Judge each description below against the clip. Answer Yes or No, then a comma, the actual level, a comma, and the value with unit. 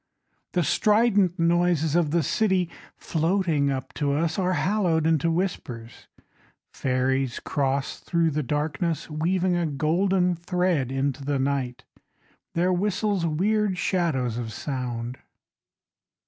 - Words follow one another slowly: Yes, slow, 120 wpm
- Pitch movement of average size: Yes, average, 4.6 semitones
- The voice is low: No, medium, 165 Hz